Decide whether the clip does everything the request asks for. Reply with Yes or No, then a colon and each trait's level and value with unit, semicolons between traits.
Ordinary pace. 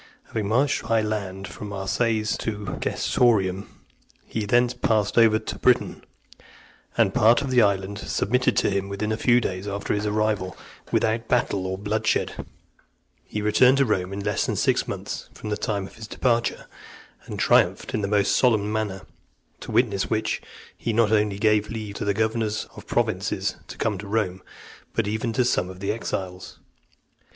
Yes: average, 175 wpm